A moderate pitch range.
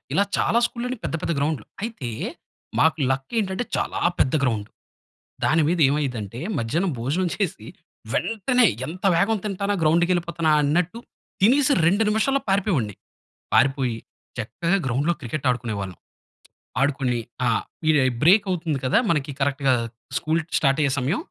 No: wide, 6.4 semitones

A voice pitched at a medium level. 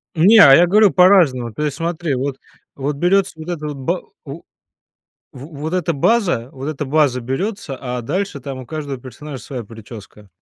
Yes: medium, 145 Hz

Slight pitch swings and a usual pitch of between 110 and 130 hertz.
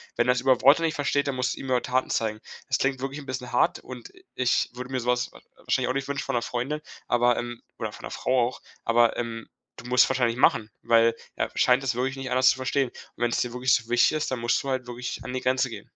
Yes: narrow, 1.6 semitones; low, 125 Hz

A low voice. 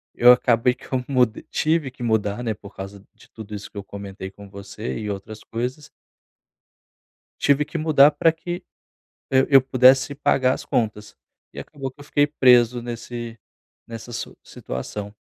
Yes: low, 120 Hz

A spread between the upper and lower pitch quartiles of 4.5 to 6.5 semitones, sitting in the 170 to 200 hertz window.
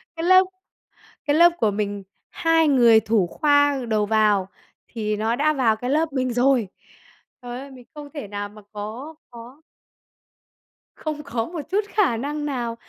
No: average, 5.3 semitones; very high, 250 Hz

